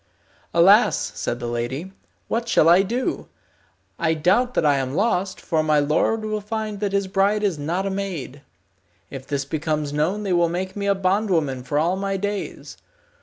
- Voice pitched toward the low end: No, medium, 185 Hz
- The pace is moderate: Yes, average, 180 wpm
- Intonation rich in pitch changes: No, average, 5.0 semitones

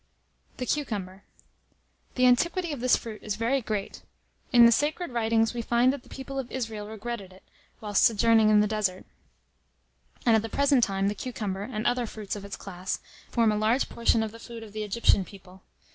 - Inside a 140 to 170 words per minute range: No, average, 195 wpm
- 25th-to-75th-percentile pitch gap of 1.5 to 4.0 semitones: Yes, average, 2.9 semitones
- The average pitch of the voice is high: Yes, high, 225 Hz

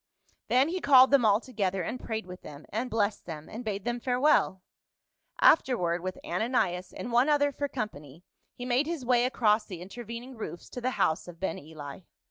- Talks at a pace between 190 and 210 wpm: Yes, average, 195 wpm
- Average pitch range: No, wide, 5.7 semitones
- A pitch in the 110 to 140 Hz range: No, high, 220 Hz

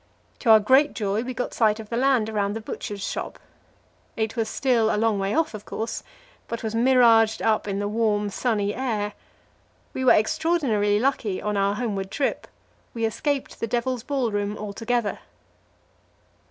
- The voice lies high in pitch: Yes, high, 220 Hz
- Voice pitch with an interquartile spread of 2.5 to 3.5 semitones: Yes, average, 2.9 semitones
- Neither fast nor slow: Yes, average, 165 wpm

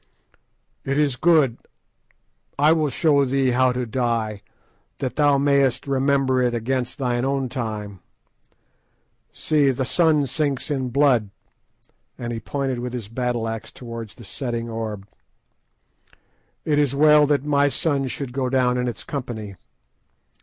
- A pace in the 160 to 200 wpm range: No, average, 140 wpm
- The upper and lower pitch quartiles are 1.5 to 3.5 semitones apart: Yes, average, 2.9 semitones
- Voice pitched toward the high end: No, low, 130 Hz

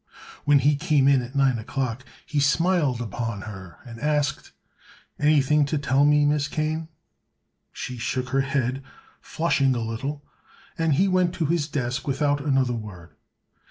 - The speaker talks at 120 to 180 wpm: Yes, average, 155 wpm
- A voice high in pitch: No, medium, 140 Hz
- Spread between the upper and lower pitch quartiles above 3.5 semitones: No, average, 3.2 semitones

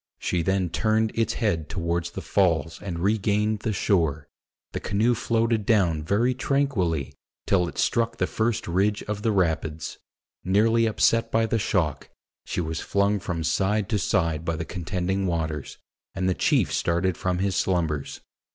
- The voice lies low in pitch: Yes, very low, 95 Hz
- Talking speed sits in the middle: Yes, average, 160 wpm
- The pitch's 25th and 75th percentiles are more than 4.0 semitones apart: Yes, average, 4.5 semitones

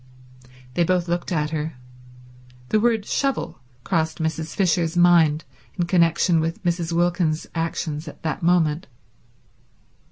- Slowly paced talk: Yes, slow, 125 wpm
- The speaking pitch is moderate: Yes, medium, 170 Hz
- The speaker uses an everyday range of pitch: No, narrow, 1.7 semitones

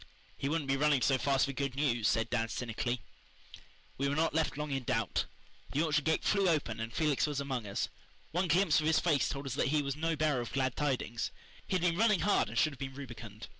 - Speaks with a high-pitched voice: No, medium, 140 Hz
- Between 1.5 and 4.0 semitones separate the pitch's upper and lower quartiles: Yes, average, 3.5 semitones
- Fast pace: Yes, fast, 240 wpm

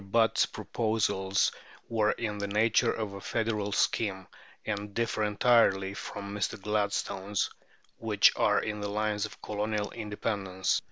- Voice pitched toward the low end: Yes, low, 105 Hz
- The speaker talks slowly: Yes, slow, 130 wpm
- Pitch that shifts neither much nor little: No, narrow, 1.4 semitones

